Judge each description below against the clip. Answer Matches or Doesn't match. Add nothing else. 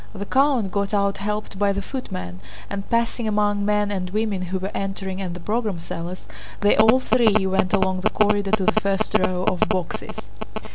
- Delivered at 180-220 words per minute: Matches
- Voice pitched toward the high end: Matches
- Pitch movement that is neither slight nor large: Doesn't match